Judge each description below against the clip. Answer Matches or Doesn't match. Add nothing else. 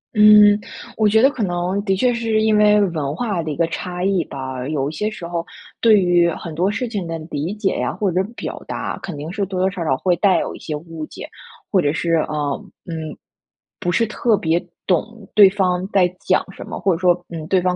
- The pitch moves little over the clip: Doesn't match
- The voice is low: Doesn't match